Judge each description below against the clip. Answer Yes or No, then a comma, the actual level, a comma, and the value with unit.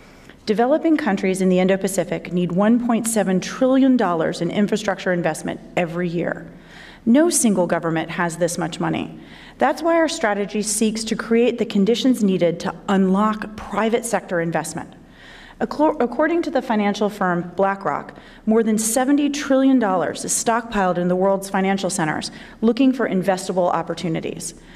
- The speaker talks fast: No, average, 140 wpm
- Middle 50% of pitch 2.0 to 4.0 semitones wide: No, average, 4.7 semitones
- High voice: Yes, high, 205 Hz